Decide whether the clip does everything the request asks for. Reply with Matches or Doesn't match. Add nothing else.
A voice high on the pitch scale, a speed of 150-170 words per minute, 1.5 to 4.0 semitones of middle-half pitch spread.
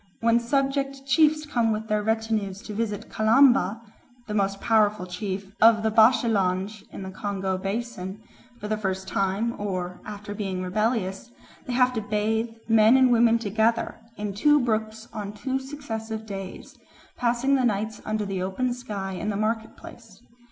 Matches